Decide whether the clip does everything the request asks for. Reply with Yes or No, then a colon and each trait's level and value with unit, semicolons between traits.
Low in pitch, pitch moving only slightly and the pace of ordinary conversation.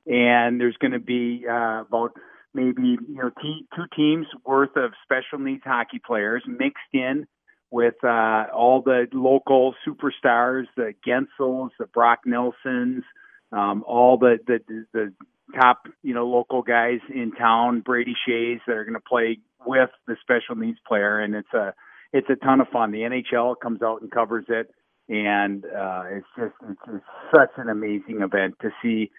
Yes: low, 120 Hz; narrow, 2.3 semitones; average, 170 wpm